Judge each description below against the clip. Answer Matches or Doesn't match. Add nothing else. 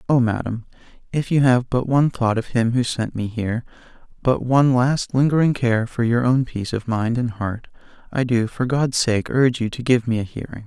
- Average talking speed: Doesn't match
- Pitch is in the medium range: Doesn't match